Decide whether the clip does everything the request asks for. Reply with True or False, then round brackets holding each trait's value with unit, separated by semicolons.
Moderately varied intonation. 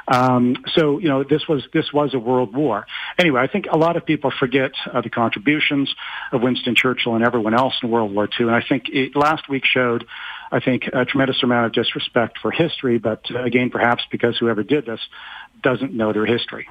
True (3.4 semitones)